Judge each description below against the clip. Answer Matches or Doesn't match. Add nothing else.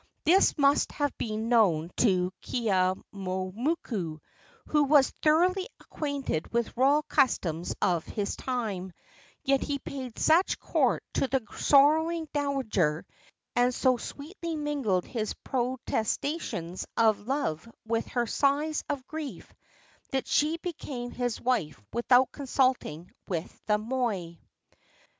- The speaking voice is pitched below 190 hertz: Doesn't match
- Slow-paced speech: Matches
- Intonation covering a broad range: Matches